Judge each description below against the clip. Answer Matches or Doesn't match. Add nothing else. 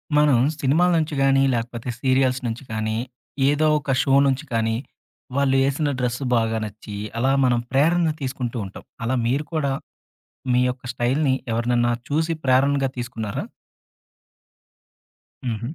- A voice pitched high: Doesn't match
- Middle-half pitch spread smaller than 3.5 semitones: Matches